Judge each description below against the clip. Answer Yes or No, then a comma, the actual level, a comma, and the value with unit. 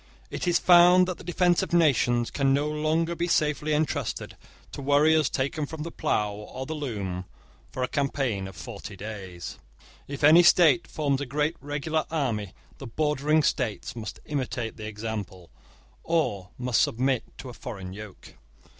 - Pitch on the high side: No, medium, 140 Hz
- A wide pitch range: Yes, wide, 6.0 semitones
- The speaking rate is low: No, average, 165 wpm